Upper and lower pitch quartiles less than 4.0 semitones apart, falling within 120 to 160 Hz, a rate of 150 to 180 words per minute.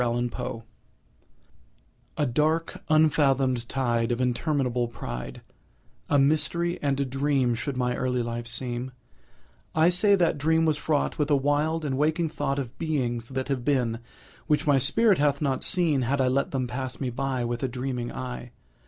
Yes: average, 3.3 semitones; low, 135 Hz; average, 165 wpm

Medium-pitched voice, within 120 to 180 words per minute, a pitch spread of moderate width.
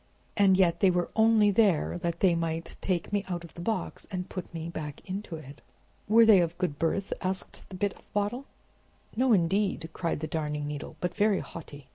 No: medium, 180 Hz; average, 200 wpm; average, 3.5 semitones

